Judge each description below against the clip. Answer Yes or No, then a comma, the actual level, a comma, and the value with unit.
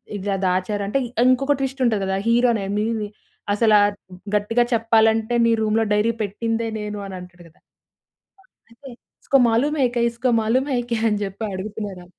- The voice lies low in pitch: No, high, 220 Hz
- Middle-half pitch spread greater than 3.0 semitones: No, average, 2.7 semitones